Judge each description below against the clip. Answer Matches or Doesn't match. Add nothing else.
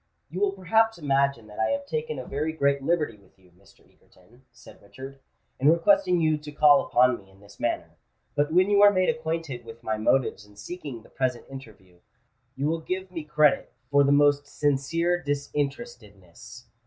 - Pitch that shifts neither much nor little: Doesn't match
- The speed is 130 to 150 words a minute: Doesn't match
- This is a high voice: Doesn't match